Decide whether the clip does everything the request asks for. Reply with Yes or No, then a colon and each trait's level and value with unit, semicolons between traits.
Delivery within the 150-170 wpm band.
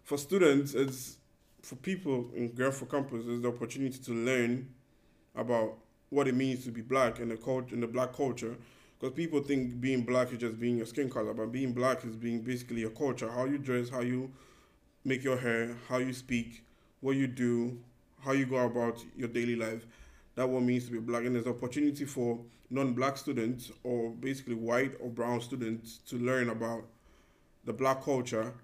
No: average, 195 wpm